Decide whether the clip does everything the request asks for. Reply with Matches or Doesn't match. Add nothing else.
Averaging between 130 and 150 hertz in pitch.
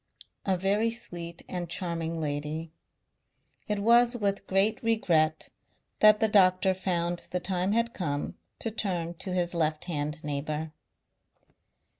Doesn't match